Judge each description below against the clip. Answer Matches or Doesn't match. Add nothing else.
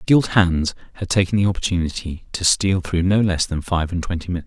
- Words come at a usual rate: Doesn't match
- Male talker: Matches